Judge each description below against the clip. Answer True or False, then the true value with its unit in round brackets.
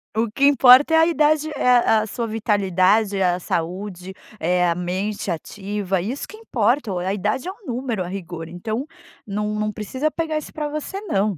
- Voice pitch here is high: True (215 Hz)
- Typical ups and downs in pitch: False (6.0 semitones)